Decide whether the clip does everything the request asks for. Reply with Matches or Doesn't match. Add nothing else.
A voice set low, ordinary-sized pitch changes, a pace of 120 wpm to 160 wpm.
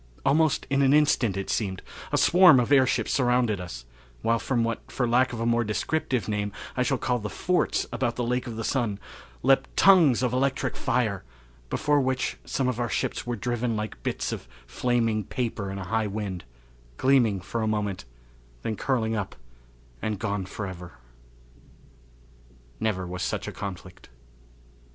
Doesn't match